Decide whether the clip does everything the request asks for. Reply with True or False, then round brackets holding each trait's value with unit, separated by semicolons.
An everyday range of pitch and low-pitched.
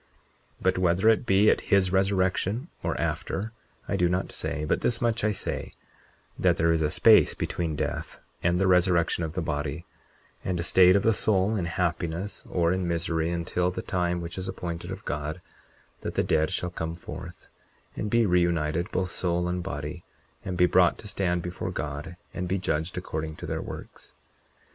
False (2.1 semitones; 90 Hz)